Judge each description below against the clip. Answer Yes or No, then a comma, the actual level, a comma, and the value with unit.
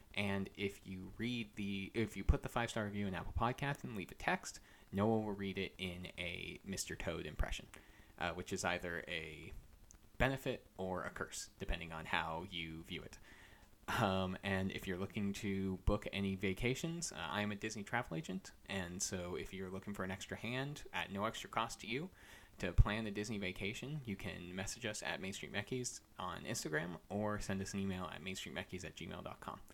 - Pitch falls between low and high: No, low, 100 Hz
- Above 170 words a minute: Yes, average, 200 wpm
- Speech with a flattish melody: Yes, narrow, 2.2 semitones